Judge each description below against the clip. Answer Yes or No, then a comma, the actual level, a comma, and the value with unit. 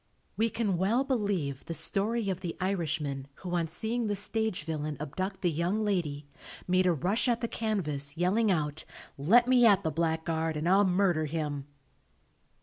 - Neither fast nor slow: Yes, average, 170 wpm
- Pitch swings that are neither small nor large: Yes, average, 4.8 semitones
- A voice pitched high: No, medium, 180 Hz